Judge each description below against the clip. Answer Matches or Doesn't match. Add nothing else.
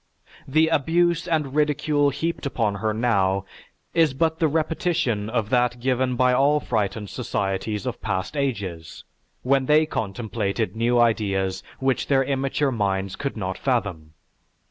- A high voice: Doesn't match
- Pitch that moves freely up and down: Matches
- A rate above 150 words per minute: Doesn't match